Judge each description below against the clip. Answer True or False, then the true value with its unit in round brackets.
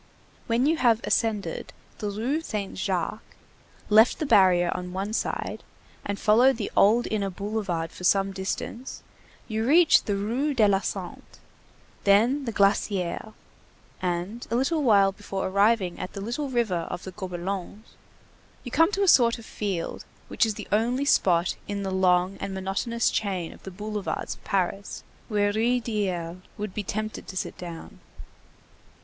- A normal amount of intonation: True (3.5 semitones)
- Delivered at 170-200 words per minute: False (160 wpm)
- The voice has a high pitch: True (205 Hz)